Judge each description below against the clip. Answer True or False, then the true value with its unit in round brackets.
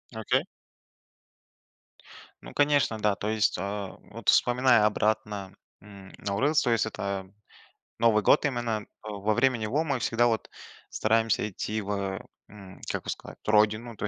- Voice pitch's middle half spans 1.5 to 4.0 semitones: True (2.5 semitones)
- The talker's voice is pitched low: True (110 Hz)